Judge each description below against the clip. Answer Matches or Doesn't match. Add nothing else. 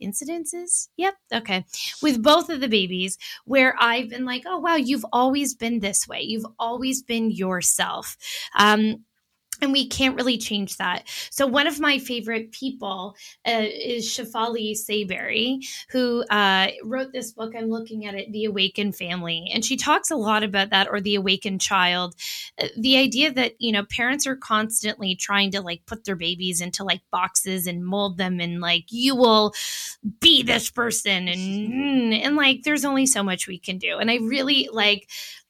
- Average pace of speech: Matches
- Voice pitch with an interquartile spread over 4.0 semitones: Matches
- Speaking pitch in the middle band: Doesn't match